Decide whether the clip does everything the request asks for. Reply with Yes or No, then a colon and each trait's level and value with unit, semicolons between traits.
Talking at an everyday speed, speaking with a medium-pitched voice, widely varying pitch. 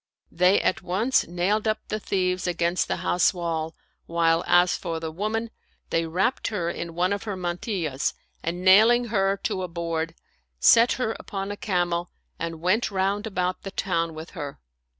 No: average, 170 wpm; medium, 180 Hz; average, 3.2 semitones